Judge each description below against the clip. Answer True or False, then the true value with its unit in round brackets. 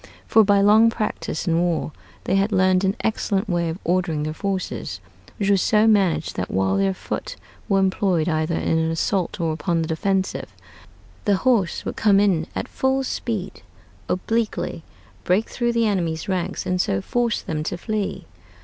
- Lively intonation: False (4.1 semitones)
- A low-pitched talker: False (190 Hz)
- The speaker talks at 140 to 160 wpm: False (175 wpm)